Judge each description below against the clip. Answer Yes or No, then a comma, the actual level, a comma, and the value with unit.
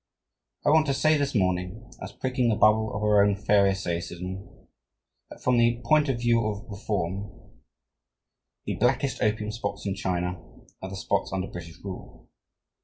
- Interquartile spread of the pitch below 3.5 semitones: No, average, 3.9 semitones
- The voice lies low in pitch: Yes, low, 105 Hz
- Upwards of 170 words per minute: No, average, 160 wpm